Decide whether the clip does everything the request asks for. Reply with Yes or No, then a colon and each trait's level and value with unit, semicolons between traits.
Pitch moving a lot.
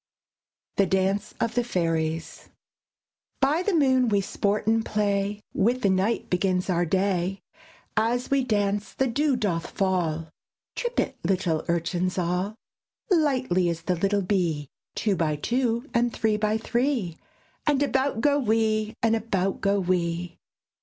No: average, 4.6 semitones